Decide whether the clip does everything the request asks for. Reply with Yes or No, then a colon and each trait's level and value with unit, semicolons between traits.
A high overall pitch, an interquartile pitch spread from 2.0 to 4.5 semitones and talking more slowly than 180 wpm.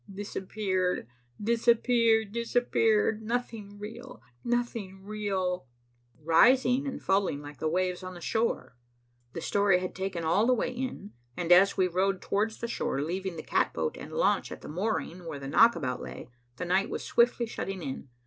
Yes: high, 195 Hz; average, 4.2 semitones; average, 160 wpm